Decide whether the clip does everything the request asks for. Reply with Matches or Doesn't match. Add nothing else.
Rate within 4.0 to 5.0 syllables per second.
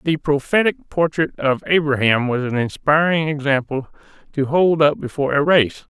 Matches